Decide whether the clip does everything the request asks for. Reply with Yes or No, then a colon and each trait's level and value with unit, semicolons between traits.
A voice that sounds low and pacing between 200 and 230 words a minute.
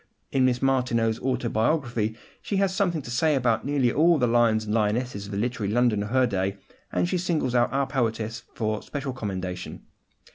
No: low, 120 Hz; average, 185 wpm